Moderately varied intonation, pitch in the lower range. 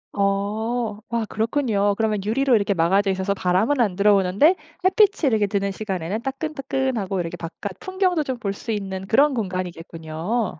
No: average, 4.2 semitones; high, 205 Hz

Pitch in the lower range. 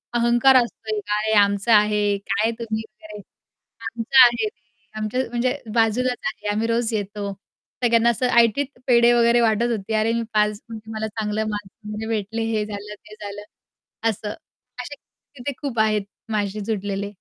No: high, 220 Hz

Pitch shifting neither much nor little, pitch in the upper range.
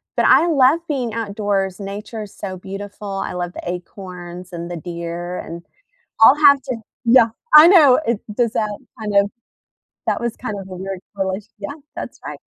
Yes: average, 4.4 semitones; high, 200 Hz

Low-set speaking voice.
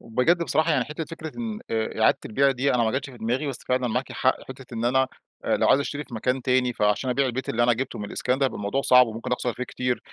Yes: low, 125 Hz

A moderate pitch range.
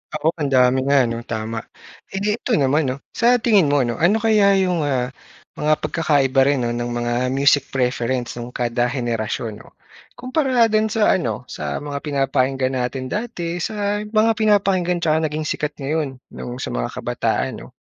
No: wide, 7.4 semitones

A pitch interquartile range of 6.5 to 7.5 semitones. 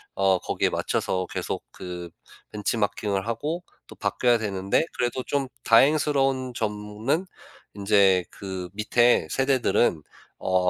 No: average, 5.1 semitones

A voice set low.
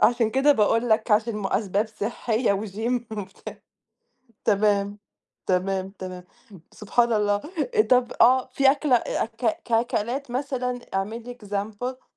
No: high, 225 Hz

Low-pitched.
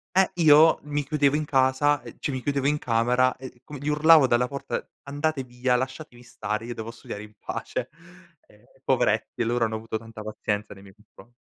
Yes: low, 130 Hz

